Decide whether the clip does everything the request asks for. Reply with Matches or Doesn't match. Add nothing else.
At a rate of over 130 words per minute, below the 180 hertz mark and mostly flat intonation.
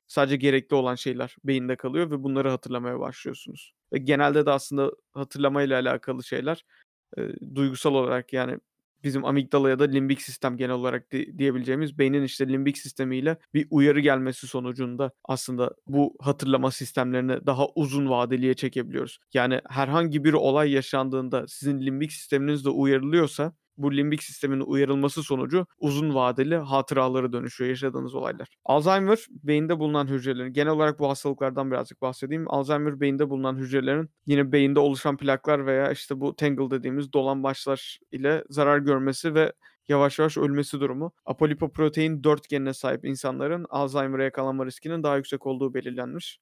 Matches